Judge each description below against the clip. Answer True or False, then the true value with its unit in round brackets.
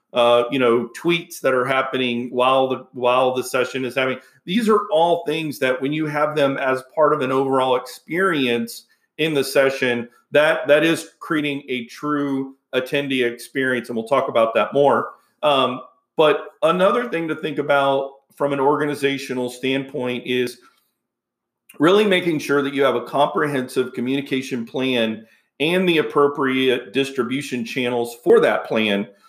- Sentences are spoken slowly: False (155 wpm)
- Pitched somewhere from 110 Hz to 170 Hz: True (135 Hz)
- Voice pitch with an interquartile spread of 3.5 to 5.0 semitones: False (2.9 semitones)